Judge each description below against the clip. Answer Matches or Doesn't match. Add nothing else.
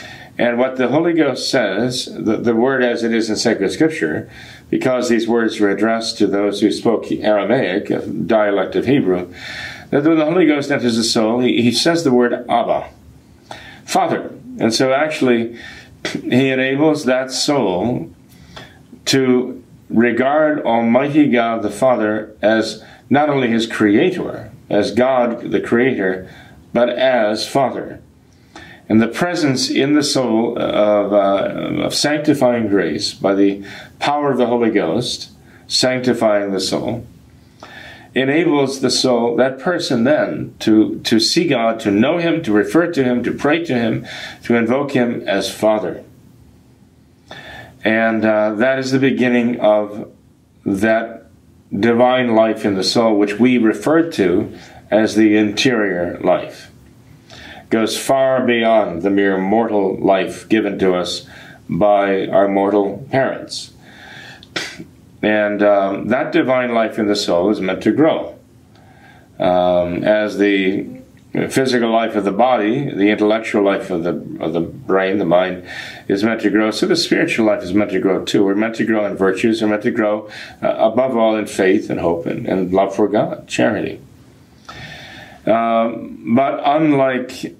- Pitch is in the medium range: Doesn't match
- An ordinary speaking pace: Matches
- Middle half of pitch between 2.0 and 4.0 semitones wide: Matches